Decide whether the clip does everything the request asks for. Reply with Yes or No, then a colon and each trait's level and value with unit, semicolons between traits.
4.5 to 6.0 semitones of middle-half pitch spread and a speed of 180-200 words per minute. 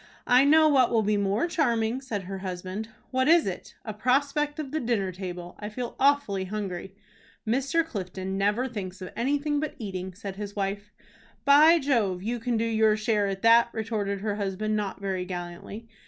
Yes: average, 5.0 semitones; average, 185 wpm